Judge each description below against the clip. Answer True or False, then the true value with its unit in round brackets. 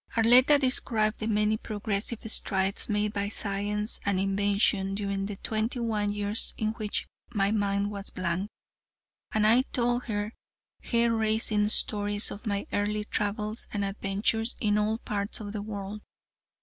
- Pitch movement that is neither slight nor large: False (1.5 semitones)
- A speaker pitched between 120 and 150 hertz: False (210 Hz)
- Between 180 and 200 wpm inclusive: False (150 wpm)